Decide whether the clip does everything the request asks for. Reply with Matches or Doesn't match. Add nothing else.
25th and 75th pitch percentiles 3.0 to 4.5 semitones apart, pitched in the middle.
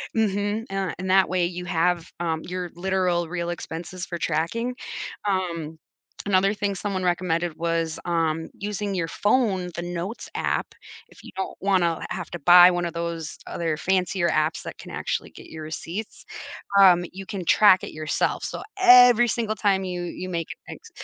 Doesn't match